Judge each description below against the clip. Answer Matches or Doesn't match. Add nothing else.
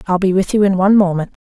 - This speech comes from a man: Doesn't match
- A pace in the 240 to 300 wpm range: Matches